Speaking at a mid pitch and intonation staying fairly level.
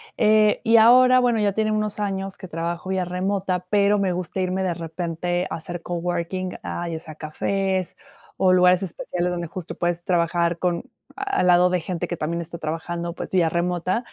Yes: medium, 180 Hz; narrow, 2.2 semitones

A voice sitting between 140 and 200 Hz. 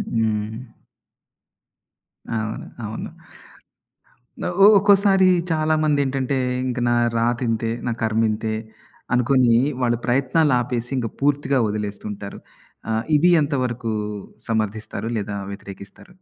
No: low, 120 Hz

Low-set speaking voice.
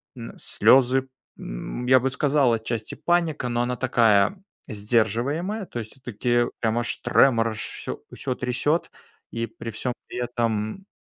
Yes: low, 120 Hz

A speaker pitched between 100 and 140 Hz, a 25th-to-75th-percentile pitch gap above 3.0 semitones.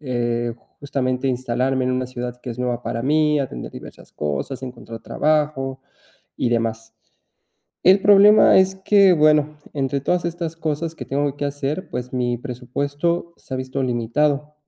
Yes: low, 135 Hz; average, 3.7 semitones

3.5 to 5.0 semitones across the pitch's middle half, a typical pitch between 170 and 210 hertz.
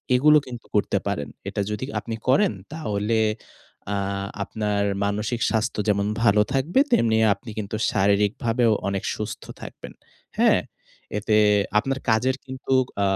No: average, 3.9 semitones; low, 110 Hz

